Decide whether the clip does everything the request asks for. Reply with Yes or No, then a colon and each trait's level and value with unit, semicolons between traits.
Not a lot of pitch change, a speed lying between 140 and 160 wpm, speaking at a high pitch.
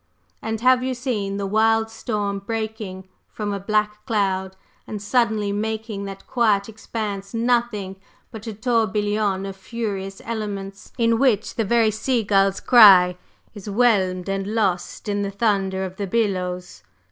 Yes: narrow, 2.3 semitones; average, 145 wpm; high, 210 Hz